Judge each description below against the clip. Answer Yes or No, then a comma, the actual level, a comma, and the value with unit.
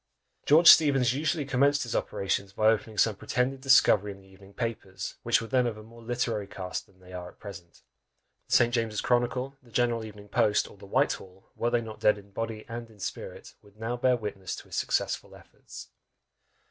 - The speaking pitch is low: Yes, low, 115 Hz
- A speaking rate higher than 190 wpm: Yes, average, 200 wpm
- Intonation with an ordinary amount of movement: Yes, average, 3.4 semitones